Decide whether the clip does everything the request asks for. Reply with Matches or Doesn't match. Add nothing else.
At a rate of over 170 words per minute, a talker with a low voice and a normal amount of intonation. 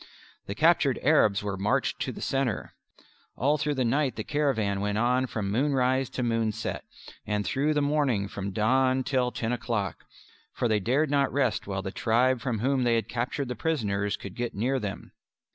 Matches